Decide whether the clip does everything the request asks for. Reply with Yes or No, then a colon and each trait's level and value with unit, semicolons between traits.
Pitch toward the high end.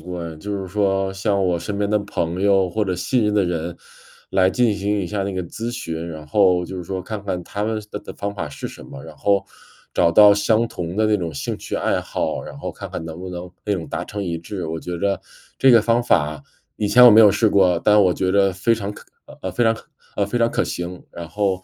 No: very low, 95 Hz